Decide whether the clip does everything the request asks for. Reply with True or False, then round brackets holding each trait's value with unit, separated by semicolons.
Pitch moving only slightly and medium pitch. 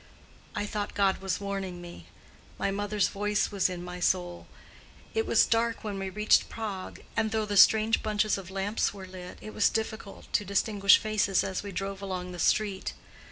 False (2.0 semitones; 200 Hz)